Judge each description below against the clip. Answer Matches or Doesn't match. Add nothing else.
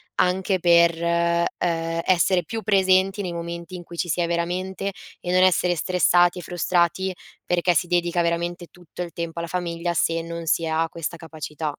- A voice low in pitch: Doesn't match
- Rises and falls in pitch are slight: Matches